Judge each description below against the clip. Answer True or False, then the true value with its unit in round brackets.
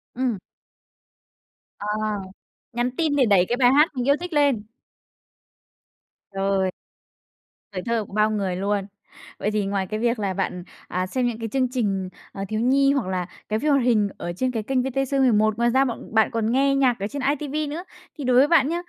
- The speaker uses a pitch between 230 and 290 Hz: True (235 Hz)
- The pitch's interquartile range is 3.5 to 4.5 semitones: False (4.9 semitones)